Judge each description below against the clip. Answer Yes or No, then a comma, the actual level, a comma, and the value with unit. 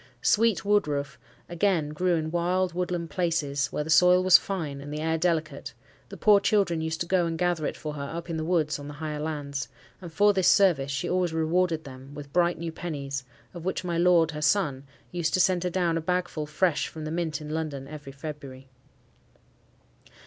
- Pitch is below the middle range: No, medium, 160 Hz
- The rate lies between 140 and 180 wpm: No, fast, 205 wpm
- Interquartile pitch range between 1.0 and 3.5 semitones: Yes, average, 3.1 semitones